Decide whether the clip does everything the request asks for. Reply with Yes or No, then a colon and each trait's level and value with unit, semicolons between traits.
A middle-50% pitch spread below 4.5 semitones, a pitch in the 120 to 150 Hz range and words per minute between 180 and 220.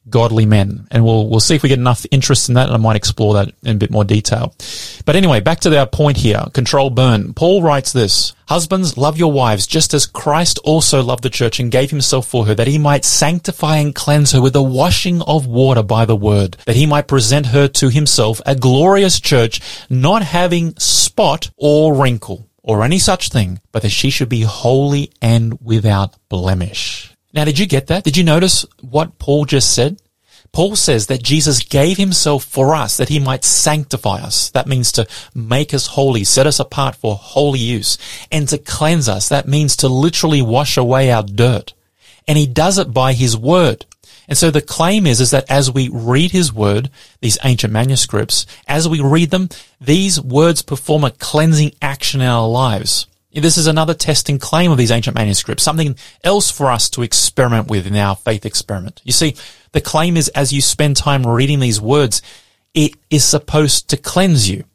No: average, 4.8 semitones; low, 135 Hz; average, 200 wpm